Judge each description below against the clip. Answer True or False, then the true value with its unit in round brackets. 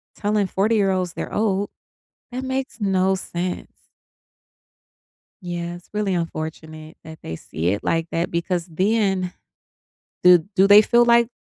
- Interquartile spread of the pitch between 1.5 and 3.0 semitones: False (3.5 semitones)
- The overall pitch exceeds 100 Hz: True (185 Hz)